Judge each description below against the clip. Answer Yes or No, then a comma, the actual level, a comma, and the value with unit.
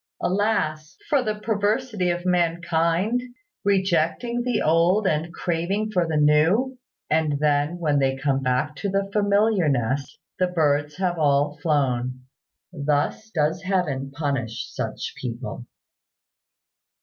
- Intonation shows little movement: No, average, 5.3 semitones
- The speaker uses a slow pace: Yes, slow, 125 wpm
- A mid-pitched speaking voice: Yes, medium, 165 Hz